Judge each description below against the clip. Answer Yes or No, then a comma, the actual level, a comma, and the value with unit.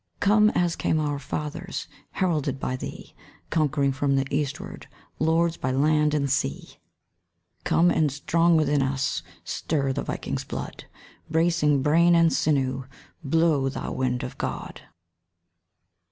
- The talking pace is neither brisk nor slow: No, slow, 130 wpm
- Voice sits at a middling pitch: Yes, medium, 150 Hz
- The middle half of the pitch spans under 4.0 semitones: Yes, average, 3.2 semitones